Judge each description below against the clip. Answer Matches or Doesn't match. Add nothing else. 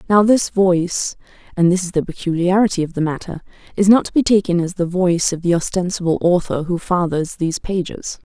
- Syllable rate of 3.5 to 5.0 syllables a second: Doesn't match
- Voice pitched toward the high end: Doesn't match